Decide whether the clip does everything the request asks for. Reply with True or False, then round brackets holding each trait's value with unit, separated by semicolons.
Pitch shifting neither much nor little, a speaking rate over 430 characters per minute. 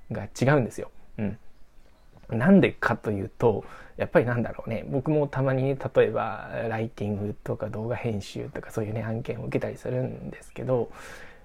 False (3.7 semitones; 355 characters per minute)